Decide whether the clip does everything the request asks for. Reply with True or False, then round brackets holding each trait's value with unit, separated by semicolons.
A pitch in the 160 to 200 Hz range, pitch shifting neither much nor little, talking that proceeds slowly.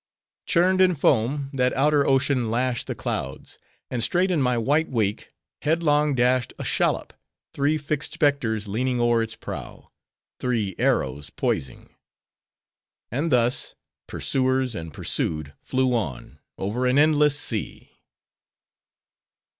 False (130 Hz; 4.3 semitones; 125 wpm)